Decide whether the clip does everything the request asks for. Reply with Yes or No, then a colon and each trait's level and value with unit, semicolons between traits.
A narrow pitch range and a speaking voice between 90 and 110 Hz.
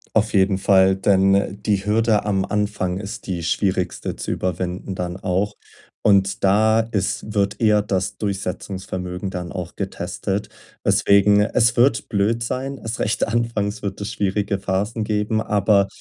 Yes: narrow, 1.9 semitones; low, 100 Hz